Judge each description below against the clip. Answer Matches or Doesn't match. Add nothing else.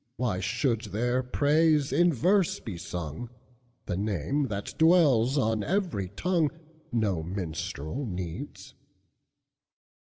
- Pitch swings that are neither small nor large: Doesn't match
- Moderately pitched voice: Doesn't match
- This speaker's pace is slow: Matches